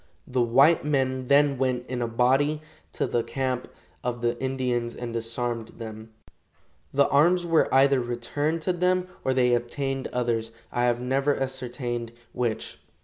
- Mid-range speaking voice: No, low, 125 Hz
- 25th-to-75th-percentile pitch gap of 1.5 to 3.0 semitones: Yes, narrow, 2.5 semitones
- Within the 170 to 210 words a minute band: No, average, 150 wpm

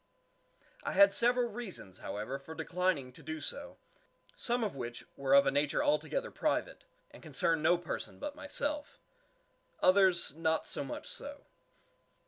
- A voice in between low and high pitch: Yes, medium, 175 Hz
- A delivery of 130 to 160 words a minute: Yes, average, 145 wpm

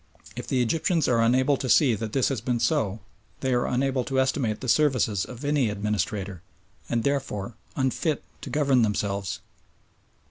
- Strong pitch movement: No, average, 4.0 semitones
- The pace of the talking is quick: No, average, 165 wpm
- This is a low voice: Yes, low, 125 Hz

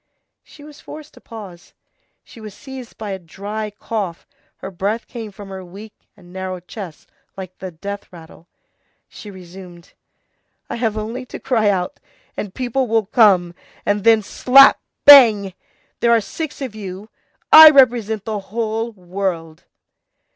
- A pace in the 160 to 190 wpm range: No, average, 150 wpm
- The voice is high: Yes, high, 210 Hz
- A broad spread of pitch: No, average, 3.5 semitones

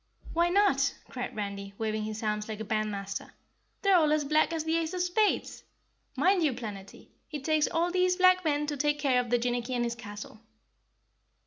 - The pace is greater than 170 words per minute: Yes, average, 190 wpm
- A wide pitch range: Yes, wide, 7.2 semitones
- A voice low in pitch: No, very high, 275 Hz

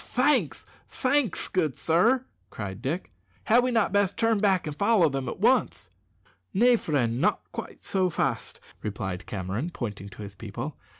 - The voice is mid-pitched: Yes, medium, 160 Hz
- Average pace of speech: Yes, average, 160 wpm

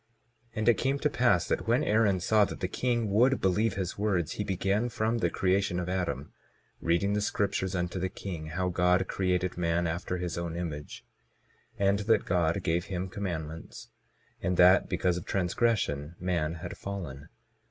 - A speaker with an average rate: Yes, average, 175 wpm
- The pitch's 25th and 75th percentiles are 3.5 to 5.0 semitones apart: No, average, 2.8 semitones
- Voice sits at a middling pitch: No, very low, 90 Hz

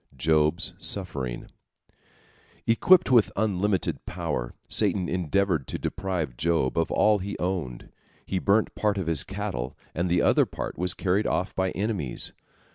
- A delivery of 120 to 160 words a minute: Yes, average, 140 wpm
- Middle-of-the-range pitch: No, very low, 90 Hz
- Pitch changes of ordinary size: Yes, average, 4.3 semitones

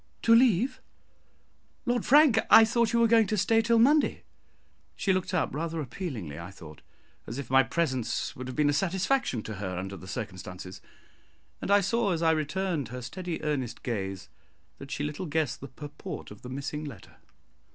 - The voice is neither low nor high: Yes, medium, 150 Hz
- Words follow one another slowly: No, average, 185 wpm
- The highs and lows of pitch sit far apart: Yes, wide, 8.9 semitones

